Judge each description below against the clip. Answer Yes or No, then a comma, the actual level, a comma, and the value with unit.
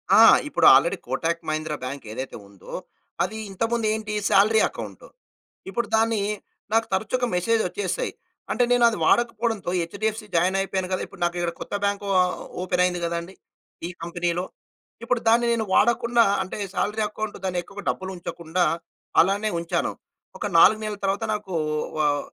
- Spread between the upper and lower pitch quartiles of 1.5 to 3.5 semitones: No, average, 4.1 semitones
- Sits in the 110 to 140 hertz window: No, high, 195 Hz